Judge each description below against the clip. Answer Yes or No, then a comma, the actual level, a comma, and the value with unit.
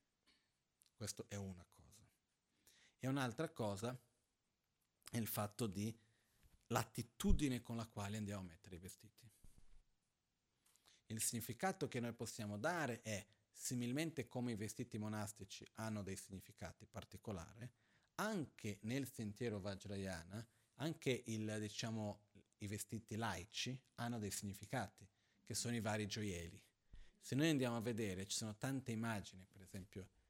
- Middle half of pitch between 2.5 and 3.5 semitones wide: Yes, average, 2.9 semitones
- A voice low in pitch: Yes, low, 110 Hz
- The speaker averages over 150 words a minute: No, average, 130 wpm